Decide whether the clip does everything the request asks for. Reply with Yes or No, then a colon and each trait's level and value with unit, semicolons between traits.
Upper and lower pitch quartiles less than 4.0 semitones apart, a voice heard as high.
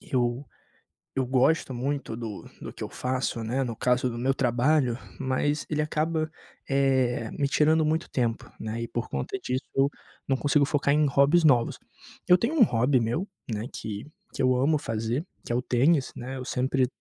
No: average, 3.4 semitones; low, 130 Hz